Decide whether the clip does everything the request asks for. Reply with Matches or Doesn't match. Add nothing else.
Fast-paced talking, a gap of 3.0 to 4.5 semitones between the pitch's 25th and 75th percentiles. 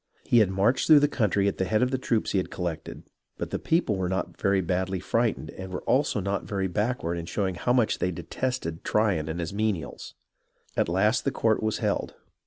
Matches